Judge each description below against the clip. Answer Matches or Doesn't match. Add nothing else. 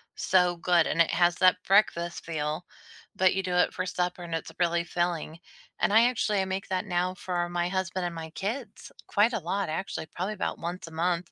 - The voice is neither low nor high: Matches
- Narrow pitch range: Matches